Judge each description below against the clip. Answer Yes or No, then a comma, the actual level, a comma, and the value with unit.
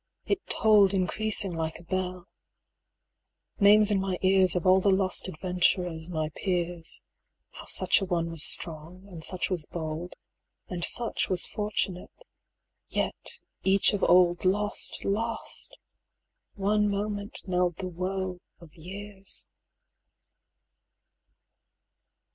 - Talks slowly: Yes, slow, 120 wpm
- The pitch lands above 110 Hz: Yes, medium, 185 Hz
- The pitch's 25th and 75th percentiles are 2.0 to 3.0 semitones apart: Yes, narrow, 2.4 semitones